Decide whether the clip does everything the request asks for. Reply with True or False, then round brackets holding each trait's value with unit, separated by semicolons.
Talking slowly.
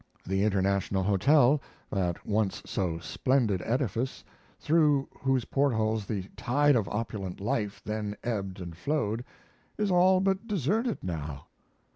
True (125 wpm)